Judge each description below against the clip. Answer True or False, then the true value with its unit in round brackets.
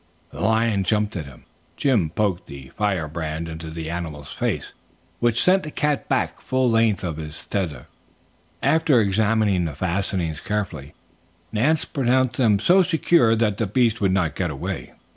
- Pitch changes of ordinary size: False (6.3 semitones)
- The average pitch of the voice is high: False (100 Hz)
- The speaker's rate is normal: True (160 wpm)